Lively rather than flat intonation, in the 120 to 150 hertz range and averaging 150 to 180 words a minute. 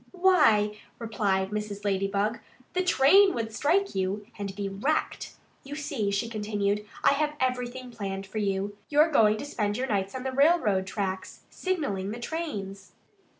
No: wide, 5.9 semitones; high, 215 Hz; average, 155 wpm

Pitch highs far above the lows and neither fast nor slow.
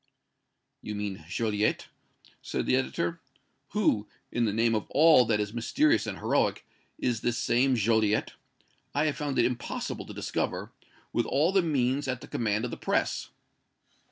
No: average, 4.7 semitones; average, 160 wpm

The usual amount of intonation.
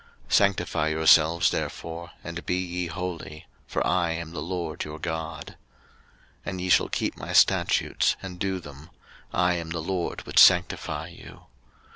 No: narrow, 2.2 semitones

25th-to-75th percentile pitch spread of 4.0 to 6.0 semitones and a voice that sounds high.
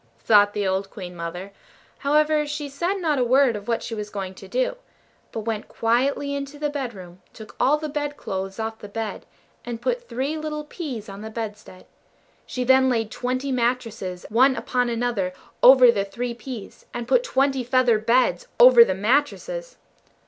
Yes: average, 5.1 semitones; high, 245 Hz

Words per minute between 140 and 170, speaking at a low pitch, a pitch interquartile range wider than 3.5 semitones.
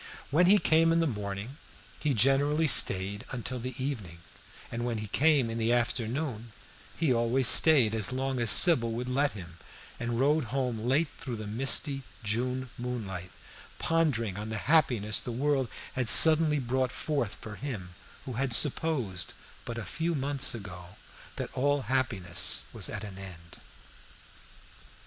Yes: average, 155 wpm; low, 125 Hz; average, 4.6 semitones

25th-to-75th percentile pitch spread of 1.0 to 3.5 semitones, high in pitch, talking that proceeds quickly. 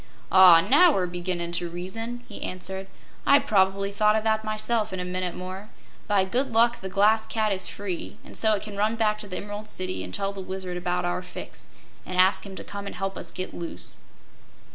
Yes: average, 2.8 semitones; high, 195 Hz; fast, 215 wpm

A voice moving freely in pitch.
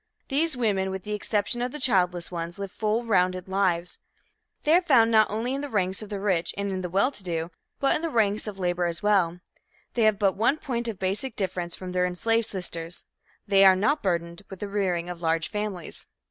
No: average, 3.8 semitones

